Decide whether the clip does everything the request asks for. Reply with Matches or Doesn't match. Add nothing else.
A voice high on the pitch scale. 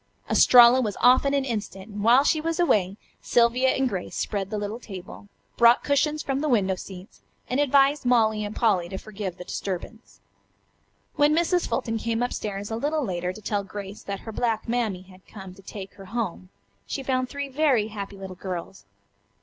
Matches